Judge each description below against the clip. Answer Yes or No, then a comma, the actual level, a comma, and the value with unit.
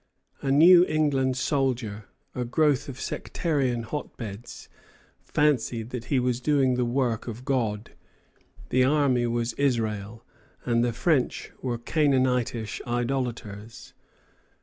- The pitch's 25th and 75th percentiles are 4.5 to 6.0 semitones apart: No, average, 2.9 semitones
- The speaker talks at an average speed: No, slow, 115 wpm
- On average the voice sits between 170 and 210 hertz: No, low, 125 Hz